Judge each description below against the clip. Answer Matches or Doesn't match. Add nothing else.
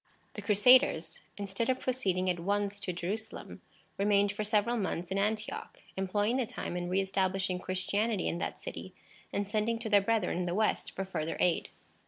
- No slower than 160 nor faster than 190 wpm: Matches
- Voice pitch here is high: Matches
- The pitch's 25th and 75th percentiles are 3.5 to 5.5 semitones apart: Doesn't match